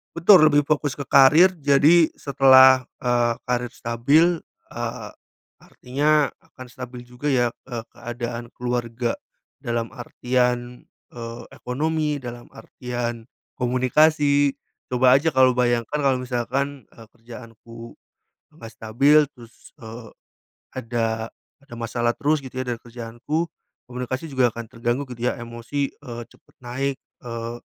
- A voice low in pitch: Yes, low, 125 Hz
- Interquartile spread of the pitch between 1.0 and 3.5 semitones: Yes, average, 2.9 semitones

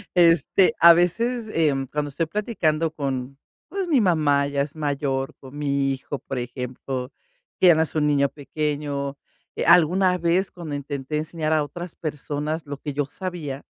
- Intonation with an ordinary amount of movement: Yes, average, 3.3 semitones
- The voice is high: No, medium, 150 Hz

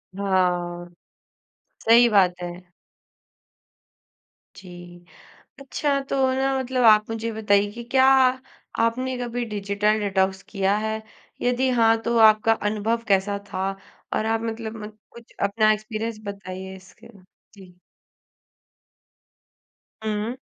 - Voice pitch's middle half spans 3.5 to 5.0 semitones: No, average, 3.1 semitones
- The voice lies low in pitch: No, high, 215 Hz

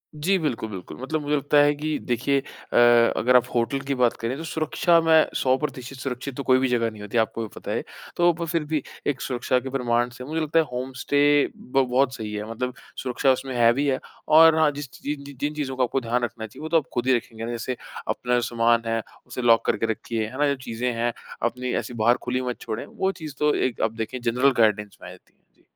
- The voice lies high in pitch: No, low, 130 Hz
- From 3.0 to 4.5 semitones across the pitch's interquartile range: Yes, average, 3.5 semitones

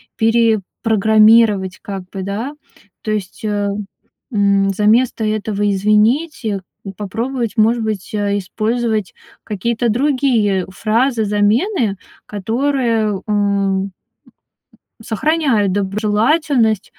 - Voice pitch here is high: Yes, high, 215 Hz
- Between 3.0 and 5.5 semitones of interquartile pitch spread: No, narrow, 2.6 semitones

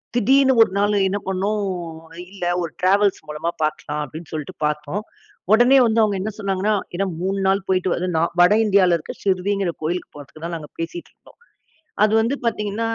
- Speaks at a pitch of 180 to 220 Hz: Yes, high, 190 Hz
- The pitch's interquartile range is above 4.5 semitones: No, average, 3.7 semitones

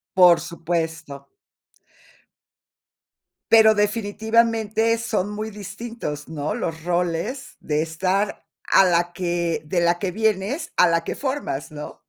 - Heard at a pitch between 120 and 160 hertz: No, medium, 185 Hz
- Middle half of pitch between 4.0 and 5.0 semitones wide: Yes, average, 4.7 semitones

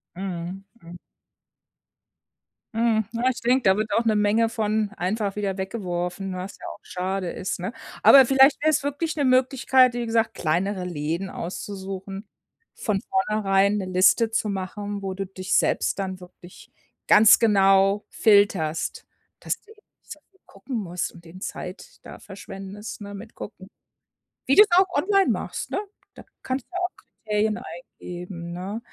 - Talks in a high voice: Yes, high, 200 Hz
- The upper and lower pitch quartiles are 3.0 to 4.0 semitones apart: Yes, average, 3.5 semitones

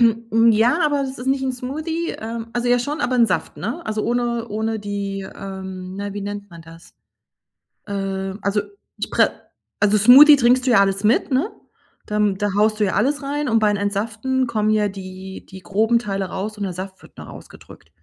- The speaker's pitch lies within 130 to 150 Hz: No, high, 215 Hz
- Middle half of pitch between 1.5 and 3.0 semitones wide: No, average, 3.7 semitones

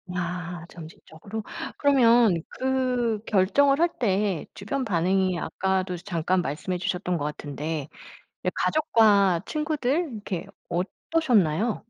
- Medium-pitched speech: No, high, 195 Hz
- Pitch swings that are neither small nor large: No, wide, 5.9 semitones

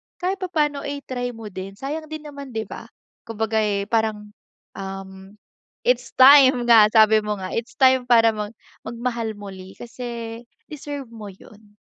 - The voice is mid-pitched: No, high, 230 Hz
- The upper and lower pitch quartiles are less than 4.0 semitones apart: No, average, 4.4 semitones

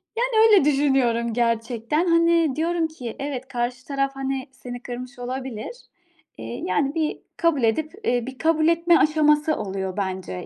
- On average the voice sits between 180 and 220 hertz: No, very high, 270 Hz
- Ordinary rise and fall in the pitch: Yes, average, 4.7 semitones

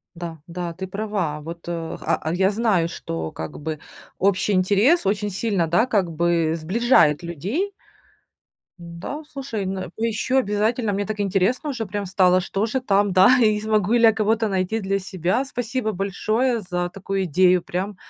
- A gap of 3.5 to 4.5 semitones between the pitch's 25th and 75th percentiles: Yes, average, 3.8 semitones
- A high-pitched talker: Yes, high, 195 Hz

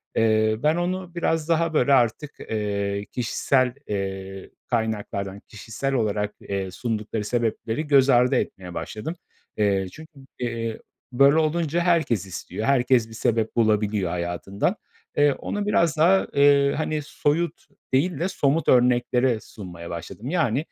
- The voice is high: No, low, 120 Hz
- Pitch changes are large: Yes, wide, 6.2 semitones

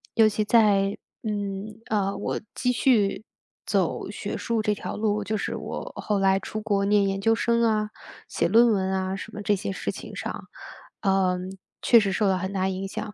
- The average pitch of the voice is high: Yes, high, 205 Hz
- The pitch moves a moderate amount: No, narrow, 1.9 semitones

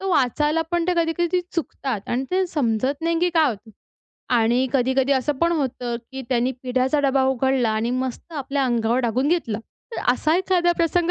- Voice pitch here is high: Yes, very high, 265 Hz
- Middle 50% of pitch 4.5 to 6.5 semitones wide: Yes, average, 5.0 semitones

